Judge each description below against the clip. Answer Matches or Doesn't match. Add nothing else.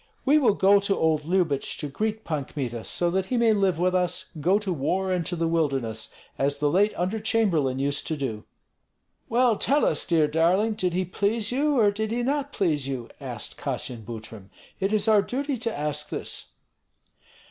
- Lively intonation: Matches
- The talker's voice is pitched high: Doesn't match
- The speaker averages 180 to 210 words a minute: Matches